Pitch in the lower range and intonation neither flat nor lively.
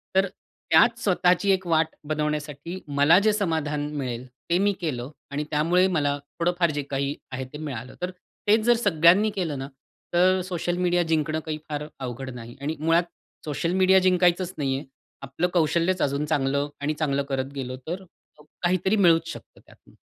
No: medium, 160 Hz; average, 4.1 semitones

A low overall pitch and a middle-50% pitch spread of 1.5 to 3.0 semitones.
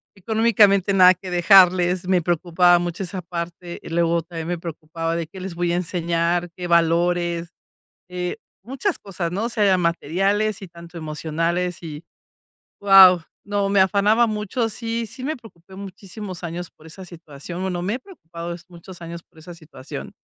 No: medium, 175 Hz; narrow, 2.6 semitones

